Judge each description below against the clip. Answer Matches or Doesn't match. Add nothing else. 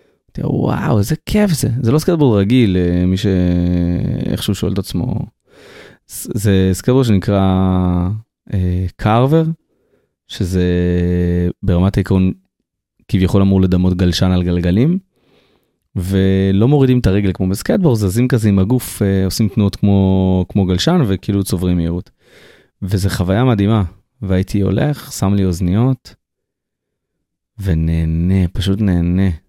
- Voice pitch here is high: Doesn't match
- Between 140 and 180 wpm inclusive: Doesn't match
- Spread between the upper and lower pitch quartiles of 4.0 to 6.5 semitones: Doesn't match